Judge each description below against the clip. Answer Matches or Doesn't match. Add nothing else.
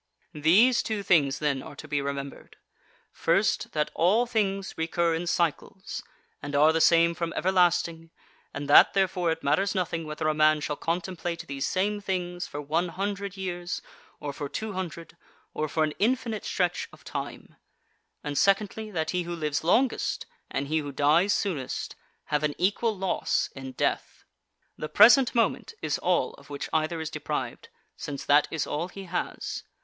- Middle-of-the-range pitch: Matches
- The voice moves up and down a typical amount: Matches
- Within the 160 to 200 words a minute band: Matches